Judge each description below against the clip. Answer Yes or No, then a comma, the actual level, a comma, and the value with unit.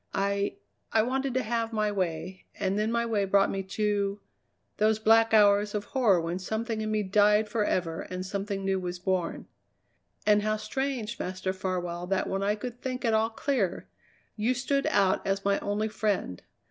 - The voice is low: No, high, 205 Hz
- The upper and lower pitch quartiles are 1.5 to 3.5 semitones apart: Yes, narrow, 2.5 semitones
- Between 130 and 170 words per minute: No, average, 180 wpm